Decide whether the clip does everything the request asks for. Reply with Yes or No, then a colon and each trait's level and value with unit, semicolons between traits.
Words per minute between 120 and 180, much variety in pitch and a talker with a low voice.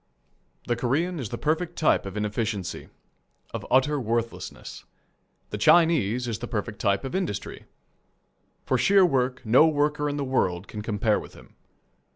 Yes: average, 155 wpm; wide, 5.9 semitones; low, 125 Hz